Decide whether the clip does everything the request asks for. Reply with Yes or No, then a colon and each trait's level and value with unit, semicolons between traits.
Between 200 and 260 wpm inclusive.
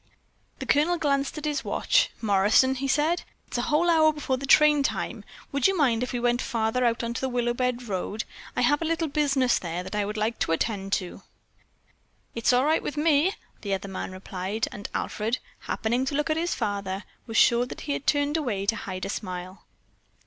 Yes: fast, 205 wpm